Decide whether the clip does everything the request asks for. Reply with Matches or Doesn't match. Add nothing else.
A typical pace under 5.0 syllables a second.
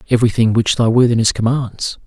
Doesn't match